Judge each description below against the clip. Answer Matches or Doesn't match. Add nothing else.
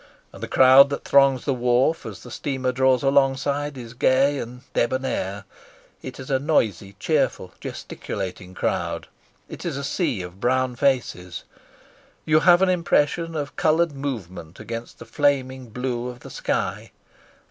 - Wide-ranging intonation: Doesn't match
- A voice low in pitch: Matches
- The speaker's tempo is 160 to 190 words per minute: Doesn't match